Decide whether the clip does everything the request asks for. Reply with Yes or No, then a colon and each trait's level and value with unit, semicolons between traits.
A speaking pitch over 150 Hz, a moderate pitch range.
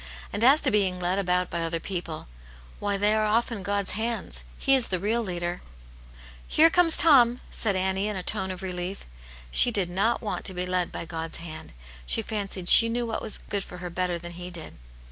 Yes: high, 190 Hz; average, 3.8 semitones